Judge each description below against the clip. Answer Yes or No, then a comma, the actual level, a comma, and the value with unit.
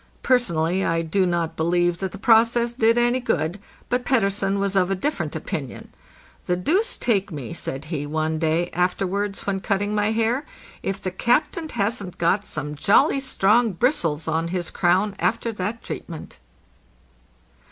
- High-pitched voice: Yes, high, 195 Hz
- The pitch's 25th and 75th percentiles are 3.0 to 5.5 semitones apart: Yes, average, 5.0 semitones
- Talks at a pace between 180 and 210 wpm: No, average, 155 wpm